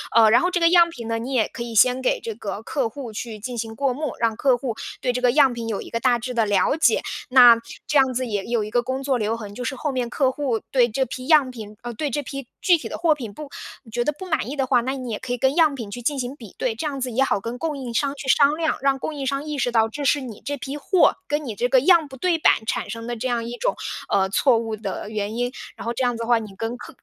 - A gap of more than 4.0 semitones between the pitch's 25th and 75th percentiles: No, average, 3.5 semitones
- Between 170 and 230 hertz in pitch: No, very high, 250 Hz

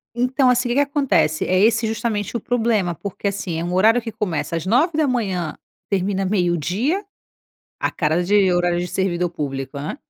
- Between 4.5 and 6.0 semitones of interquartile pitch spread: Yes, average, 5.3 semitones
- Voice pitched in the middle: No, high, 195 Hz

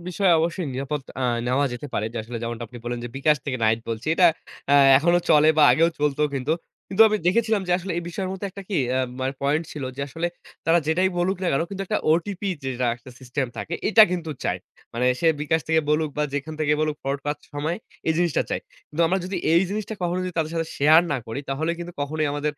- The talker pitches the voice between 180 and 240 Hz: No, medium, 155 Hz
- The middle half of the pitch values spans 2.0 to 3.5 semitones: No, average, 4.2 semitones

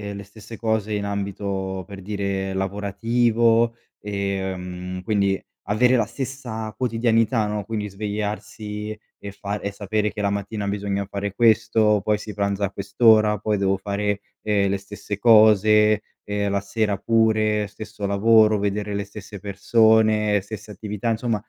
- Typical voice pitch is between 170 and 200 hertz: No, low, 105 Hz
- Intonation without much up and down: Yes, narrow, 1.5 semitones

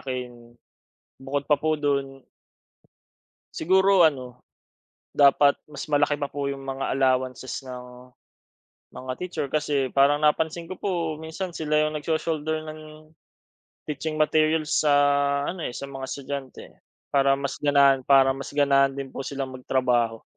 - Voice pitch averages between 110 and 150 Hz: Yes, medium, 140 Hz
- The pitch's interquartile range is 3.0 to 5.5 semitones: No, narrow, 2.6 semitones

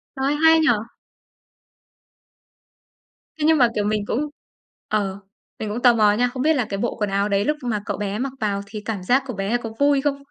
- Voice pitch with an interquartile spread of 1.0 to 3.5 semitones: No, average, 4.8 semitones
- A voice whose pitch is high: Yes, high, 225 Hz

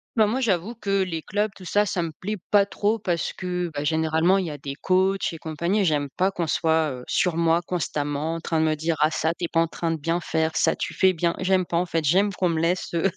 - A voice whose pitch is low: No, medium, 170 Hz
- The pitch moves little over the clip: No, average, 3.0 semitones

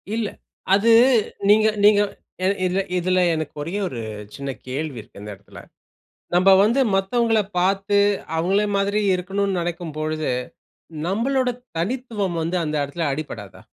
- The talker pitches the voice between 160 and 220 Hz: Yes, medium, 185 Hz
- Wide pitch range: No, average, 4.7 semitones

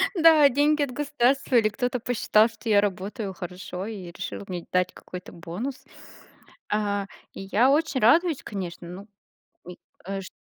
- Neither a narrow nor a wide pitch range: No, wide, 6.1 semitones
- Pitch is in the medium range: No, high, 215 Hz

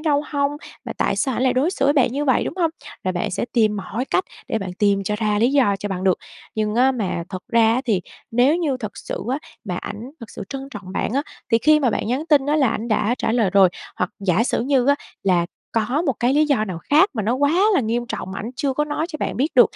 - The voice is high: Yes, high, 240 Hz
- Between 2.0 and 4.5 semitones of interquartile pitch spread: No, average, 5.3 semitones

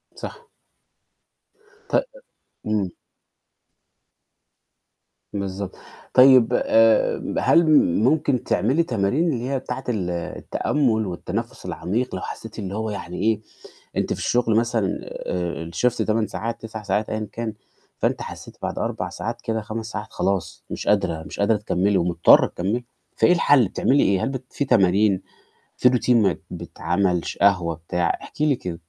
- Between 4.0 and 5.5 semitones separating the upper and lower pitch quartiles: Yes, average, 4.5 semitones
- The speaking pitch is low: Yes, low, 110 Hz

